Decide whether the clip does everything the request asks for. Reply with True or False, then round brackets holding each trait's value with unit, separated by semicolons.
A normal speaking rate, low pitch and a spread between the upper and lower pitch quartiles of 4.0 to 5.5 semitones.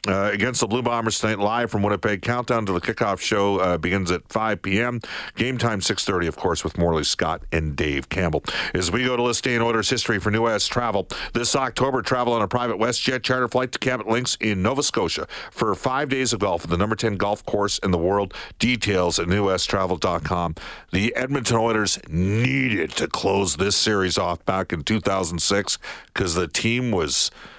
True (195 wpm; 105 Hz; 4.3 semitones)